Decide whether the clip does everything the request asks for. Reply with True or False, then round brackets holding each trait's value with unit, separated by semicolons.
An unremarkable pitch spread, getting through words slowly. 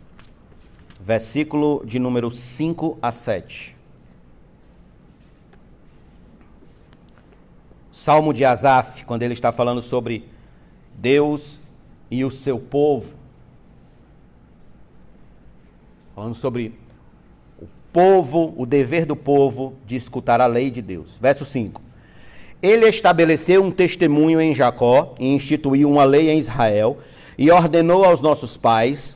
True (4.2 semitones; 105 wpm)